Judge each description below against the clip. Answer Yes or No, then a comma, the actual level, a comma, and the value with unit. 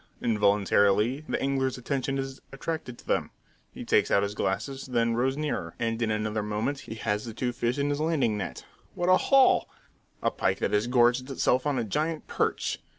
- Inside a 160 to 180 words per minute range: No, average, 195 wpm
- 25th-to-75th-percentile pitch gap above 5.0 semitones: No, average, 4.3 semitones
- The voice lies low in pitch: Yes, low, 125 Hz